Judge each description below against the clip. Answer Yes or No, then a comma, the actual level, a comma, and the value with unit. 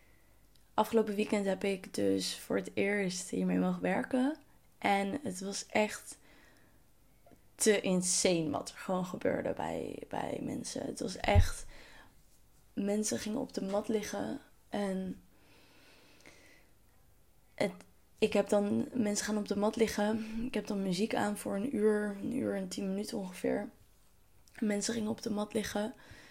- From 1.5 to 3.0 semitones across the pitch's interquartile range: Yes, narrow, 2.4 semitones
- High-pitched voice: Yes, high, 205 Hz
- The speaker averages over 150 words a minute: No, average, 145 wpm